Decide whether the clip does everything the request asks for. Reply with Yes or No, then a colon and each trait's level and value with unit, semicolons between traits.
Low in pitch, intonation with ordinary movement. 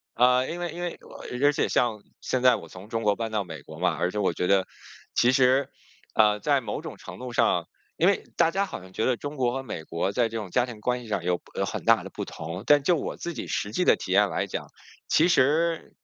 No: low, 125 Hz; wide, 5.7 semitones